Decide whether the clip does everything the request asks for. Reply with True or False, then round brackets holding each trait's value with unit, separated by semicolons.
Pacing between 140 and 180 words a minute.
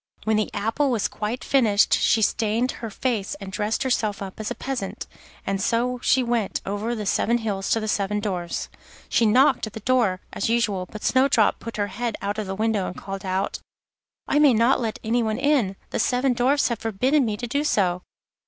False (205 wpm)